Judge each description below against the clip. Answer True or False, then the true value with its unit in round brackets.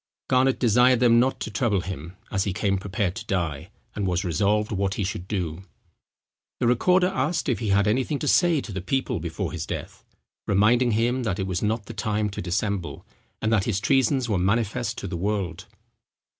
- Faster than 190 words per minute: True (200 wpm)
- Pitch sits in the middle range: False (105 Hz)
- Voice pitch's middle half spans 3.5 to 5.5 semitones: True (4.2 semitones)